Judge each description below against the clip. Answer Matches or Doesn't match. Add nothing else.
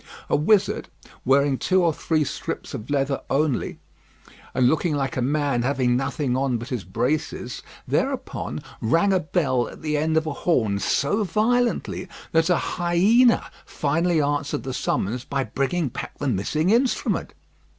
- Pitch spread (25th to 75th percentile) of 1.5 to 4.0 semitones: Doesn't match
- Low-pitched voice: Doesn't match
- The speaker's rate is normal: Matches